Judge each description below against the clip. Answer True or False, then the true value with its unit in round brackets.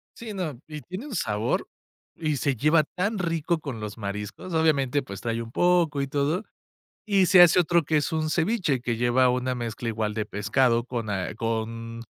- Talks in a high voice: False (135 Hz)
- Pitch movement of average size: False (6.3 semitones)